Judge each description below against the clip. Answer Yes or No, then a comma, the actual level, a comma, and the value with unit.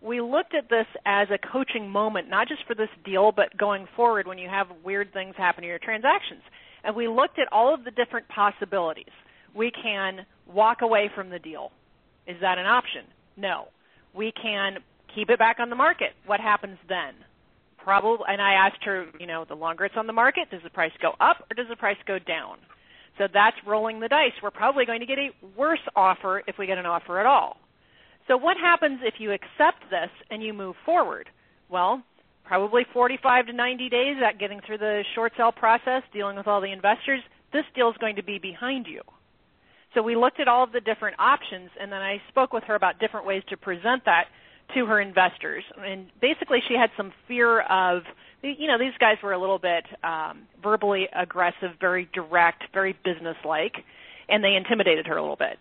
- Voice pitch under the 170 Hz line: No, high, 205 Hz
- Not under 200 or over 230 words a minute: Yes, fast, 205 wpm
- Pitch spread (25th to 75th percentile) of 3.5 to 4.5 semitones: Yes, average, 3.8 semitones